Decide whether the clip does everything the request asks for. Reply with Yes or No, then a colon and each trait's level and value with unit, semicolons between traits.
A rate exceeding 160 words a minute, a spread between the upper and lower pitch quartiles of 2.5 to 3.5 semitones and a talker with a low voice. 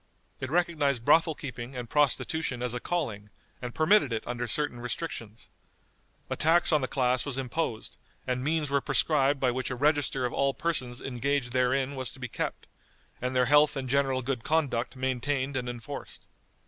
Yes: average, 175 wpm; average, 2.9 semitones; low, 130 Hz